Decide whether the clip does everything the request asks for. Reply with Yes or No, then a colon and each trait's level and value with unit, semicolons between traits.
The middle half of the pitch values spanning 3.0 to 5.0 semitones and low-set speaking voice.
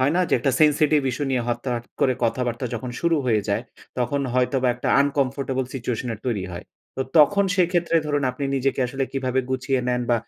No: narrow, 2.5 semitones; low, 130 Hz